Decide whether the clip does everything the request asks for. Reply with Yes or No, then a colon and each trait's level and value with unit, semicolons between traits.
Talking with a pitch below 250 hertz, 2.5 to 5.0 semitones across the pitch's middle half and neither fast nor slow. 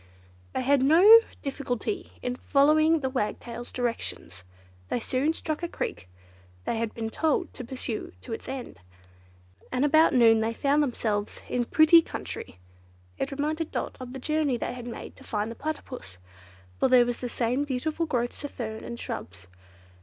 No: very high, 255 Hz; average, 4.4 semitones; average, 170 wpm